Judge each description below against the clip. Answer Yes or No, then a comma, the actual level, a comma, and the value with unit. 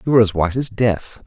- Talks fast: Yes, fast, 285 wpm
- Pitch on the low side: Yes, low, 105 Hz